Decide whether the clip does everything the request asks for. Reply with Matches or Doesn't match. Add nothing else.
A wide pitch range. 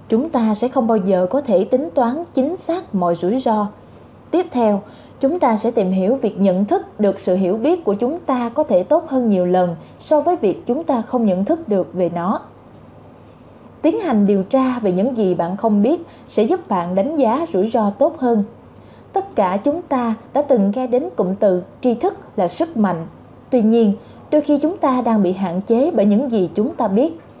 Matches